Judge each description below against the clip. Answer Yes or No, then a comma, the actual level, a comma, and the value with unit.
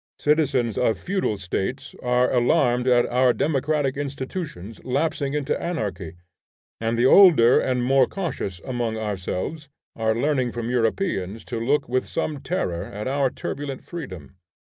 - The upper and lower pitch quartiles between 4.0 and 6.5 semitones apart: Yes, average, 4.4 semitones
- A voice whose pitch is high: No, low, 125 Hz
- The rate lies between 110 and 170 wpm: Yes, average, 140 wpm